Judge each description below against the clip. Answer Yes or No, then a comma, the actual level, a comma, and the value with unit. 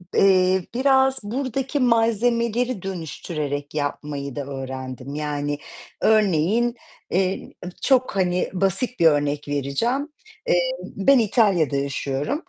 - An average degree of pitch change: No, wide, 8.7 semitones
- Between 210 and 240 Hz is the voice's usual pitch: No, high, 190 Hz